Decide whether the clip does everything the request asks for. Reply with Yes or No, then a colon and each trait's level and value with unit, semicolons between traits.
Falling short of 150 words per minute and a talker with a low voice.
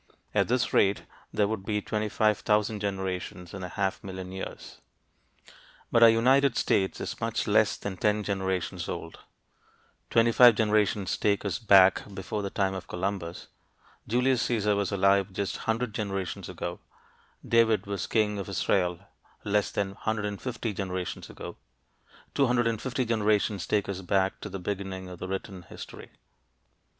Yes: average, 140 wpm; low, 100 Hz